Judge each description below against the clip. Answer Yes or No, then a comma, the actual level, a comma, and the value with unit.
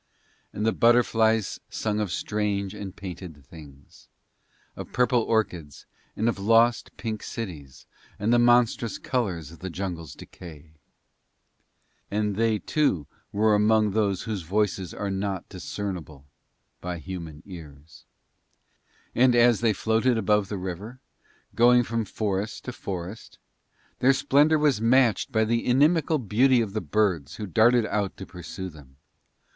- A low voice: Yes, low, 105 Hz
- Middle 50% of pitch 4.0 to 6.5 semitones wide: Yes, average, 4.3 semitones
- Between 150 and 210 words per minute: No, average, 140 wpm